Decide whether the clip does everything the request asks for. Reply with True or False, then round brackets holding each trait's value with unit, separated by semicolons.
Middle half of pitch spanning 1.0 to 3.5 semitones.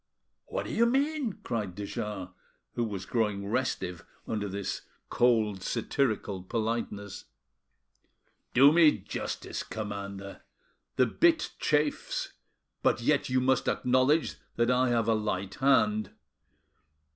False (4.4 semitones)